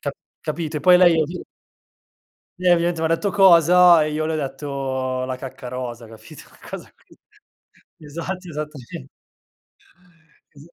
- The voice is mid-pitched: Yes, medium, 155 Hz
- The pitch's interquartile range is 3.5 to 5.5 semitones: Yes, average, 4.4 semitones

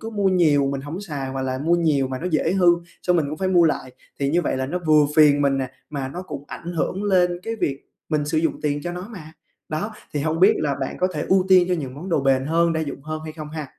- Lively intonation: No, average, 3.8 semitones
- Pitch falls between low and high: Yes, medium, 155 Hz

